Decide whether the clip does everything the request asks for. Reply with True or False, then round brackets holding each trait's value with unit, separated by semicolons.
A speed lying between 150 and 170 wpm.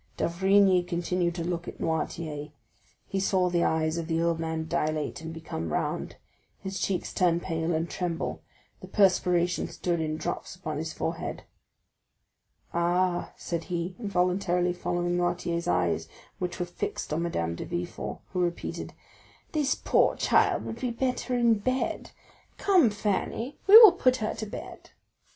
True (155 wpm)